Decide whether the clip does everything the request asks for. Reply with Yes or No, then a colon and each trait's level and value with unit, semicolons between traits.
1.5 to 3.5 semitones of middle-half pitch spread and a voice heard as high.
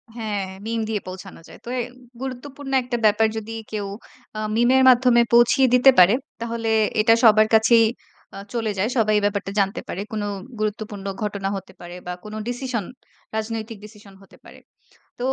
Yes: narrow, 2.6 semitones; high, 220 Hz